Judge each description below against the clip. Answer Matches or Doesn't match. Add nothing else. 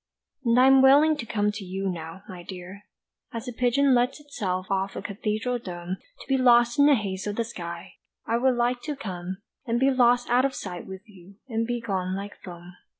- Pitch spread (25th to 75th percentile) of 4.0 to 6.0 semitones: Matches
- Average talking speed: Doesn't match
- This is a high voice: Matches